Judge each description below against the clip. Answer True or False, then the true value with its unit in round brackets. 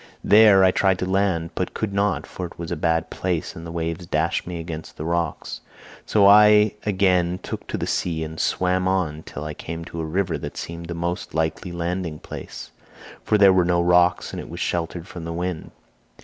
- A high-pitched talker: False (85 Hz)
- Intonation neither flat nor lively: False (2.2 semitones)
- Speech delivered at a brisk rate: True (210 wpm)